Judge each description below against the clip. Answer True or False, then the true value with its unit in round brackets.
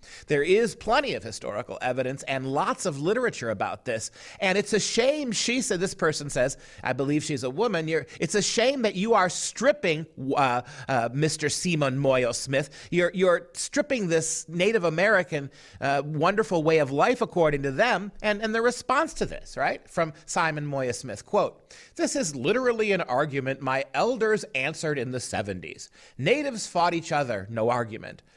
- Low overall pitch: False (165 Hz)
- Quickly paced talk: False (175 wpm)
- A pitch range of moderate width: False (7.1 semitones)